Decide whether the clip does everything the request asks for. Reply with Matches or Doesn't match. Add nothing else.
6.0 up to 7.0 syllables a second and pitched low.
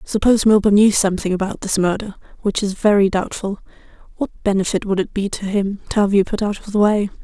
Doesn't match